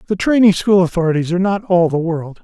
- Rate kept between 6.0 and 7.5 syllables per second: Yes, 6.3 syllables/s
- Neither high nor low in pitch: Yes, medium, 180 Hz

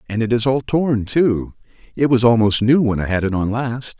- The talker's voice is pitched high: No, low, 115 Hz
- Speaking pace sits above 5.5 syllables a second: No, 5.0 syllables/s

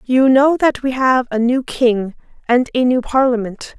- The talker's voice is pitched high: Yes, very high, 250 Hz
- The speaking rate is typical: Yes, average, 190 wpm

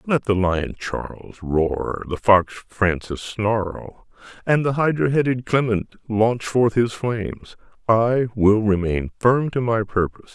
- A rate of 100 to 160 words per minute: Yes, average, 145 wpm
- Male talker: Yes, male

